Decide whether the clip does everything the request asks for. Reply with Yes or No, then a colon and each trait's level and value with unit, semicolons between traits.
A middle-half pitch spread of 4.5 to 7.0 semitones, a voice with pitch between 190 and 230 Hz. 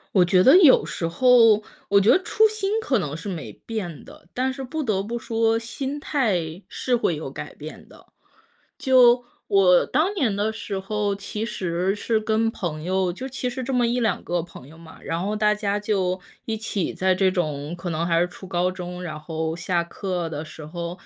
Yes: average, 5.1 semitones; high, 195 Hz